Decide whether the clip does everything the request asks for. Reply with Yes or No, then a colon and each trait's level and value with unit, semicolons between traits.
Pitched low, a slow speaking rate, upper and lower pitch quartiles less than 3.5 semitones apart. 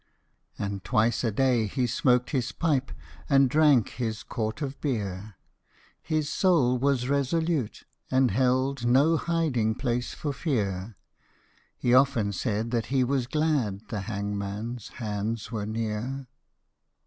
No: low, 125 Hz; slow, 130 wpm; average, 4.1 semitones